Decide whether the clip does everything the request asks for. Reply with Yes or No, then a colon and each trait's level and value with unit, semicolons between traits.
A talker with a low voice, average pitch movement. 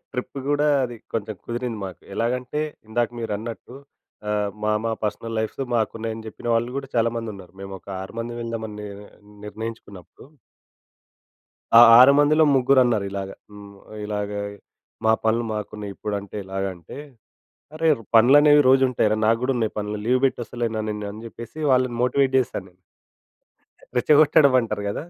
Yes: low, 115 Hz; average, 3.2 semitones